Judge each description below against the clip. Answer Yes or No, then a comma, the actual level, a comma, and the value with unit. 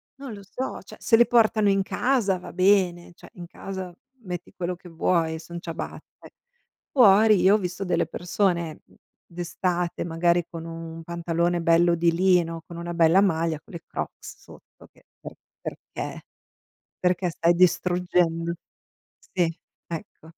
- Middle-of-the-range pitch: Yes, medium, 175 Hz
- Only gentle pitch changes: Yes, narrow, 2.1 semitones